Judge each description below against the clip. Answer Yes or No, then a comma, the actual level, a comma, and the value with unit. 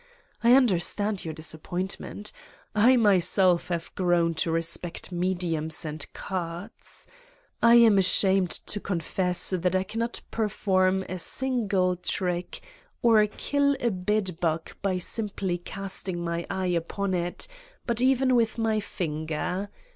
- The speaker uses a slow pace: Yes, slow, 125 wpm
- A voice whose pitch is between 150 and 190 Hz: Yes, medium, 185 Hz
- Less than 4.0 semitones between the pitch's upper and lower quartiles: Yes, average, 3.4 semitones